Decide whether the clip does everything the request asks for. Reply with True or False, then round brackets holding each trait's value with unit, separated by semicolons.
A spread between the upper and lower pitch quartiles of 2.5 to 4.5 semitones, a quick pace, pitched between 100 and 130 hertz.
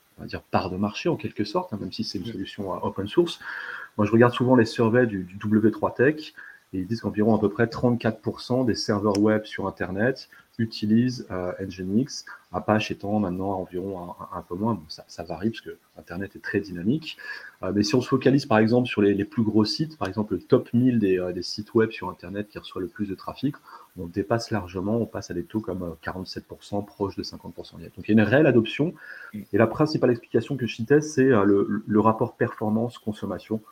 True (3.1 semitones; 230 wpm; 105 Hz)